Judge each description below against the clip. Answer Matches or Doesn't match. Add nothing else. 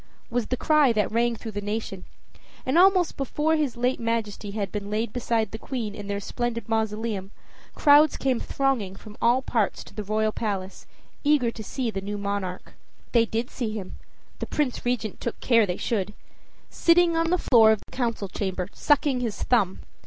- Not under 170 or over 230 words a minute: Matches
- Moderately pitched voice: Doesn't match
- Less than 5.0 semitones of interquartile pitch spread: Matches